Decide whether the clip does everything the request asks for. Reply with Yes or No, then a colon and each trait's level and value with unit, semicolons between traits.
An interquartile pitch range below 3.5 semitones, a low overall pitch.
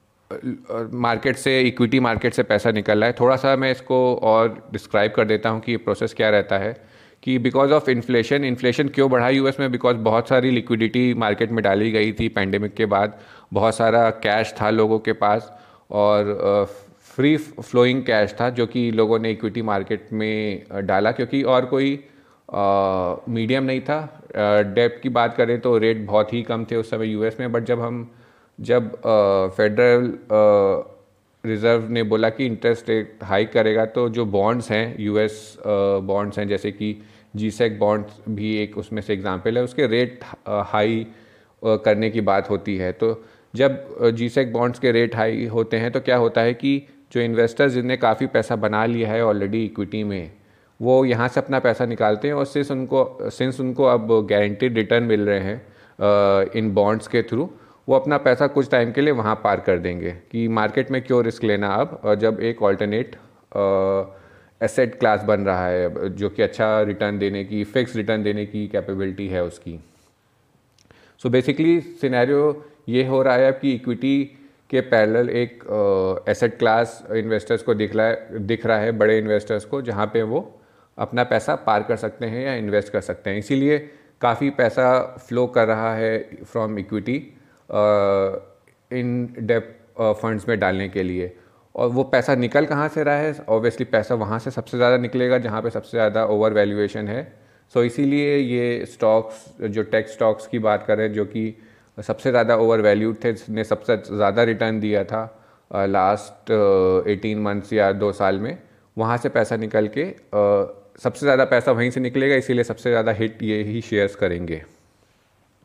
Yes: average, 2.9 semitones; low, 115 Hz